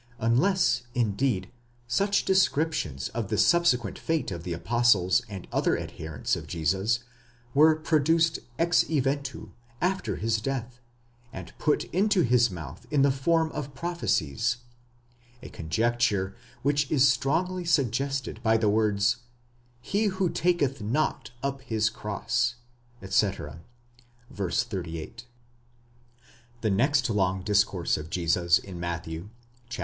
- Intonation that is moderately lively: No, wide, 7.2 semitones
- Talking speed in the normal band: No, slow, 125 wpm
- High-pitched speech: No, low, 120 Hz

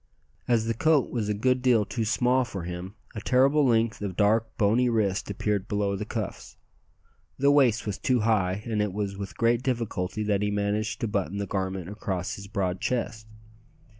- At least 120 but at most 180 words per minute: No, average, 190 wpm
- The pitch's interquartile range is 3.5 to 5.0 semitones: No, average, 2.8 semitones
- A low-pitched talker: Yes, low, 105 Hz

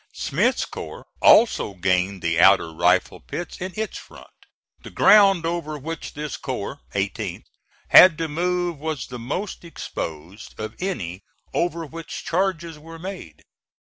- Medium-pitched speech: Yes, medium, 155 Hz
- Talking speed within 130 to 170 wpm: Yes, average, 140 wpm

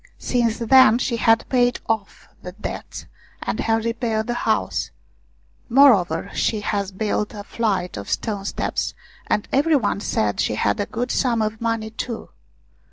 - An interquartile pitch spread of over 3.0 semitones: No, average, 2.7 semitones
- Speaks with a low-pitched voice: No, high, 220 Hz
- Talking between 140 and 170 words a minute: Yes, average, 160 wpm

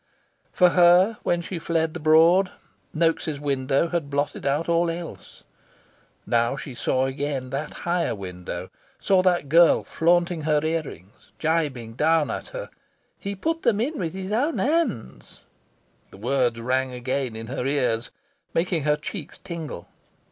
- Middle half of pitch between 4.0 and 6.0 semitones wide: Yes, average, 4.8 semitones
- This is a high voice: No, medium, 155 Hz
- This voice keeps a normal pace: Yes, average, 150 wpm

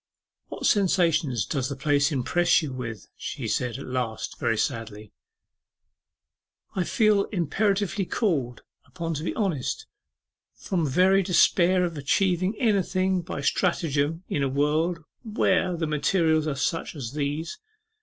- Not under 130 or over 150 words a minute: Yes, slow, 135 wpm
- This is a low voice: No, medium, 160 Hz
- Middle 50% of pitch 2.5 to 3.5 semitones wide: No, average, 4.9 semitones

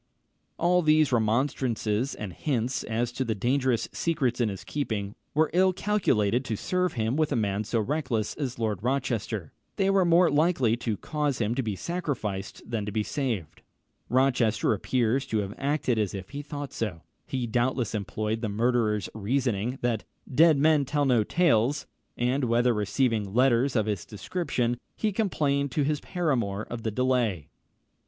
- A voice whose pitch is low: Yes, low, 120 Hz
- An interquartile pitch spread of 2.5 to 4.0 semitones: No, average, 4.7 semitones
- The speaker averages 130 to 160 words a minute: No, average, 170 wpm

